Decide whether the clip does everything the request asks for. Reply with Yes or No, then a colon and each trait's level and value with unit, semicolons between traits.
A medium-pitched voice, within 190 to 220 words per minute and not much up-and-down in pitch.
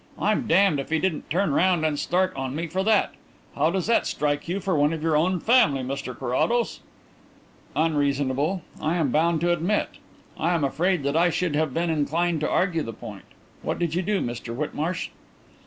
No: medium, 165 Hz; average, 195 wpm; average, 3.8 semitones